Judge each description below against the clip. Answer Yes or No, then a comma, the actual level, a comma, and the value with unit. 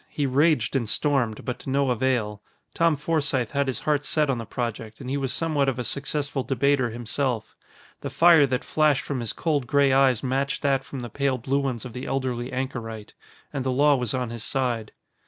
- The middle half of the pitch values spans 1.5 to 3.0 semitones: Yes, narrow, 2.6 semitones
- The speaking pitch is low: Yes, low, 130 Hz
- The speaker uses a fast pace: Yes, fast, 210 wpm